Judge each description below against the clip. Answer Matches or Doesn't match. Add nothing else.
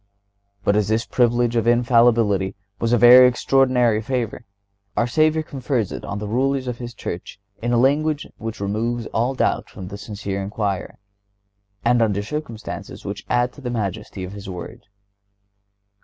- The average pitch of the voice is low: Matches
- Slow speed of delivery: Doesn't match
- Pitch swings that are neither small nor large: Matches